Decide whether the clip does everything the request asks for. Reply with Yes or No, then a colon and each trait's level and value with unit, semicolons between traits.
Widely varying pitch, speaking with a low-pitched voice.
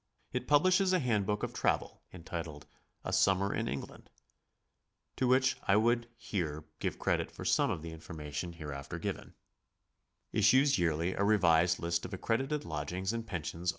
Yes: wide, 6.1 semitones; very low, 95 Hz